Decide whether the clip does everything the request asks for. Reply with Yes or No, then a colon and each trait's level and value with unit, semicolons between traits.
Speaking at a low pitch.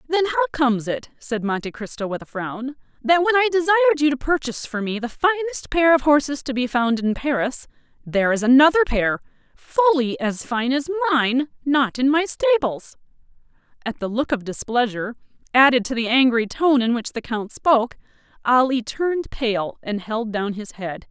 No: very high, 265 Hz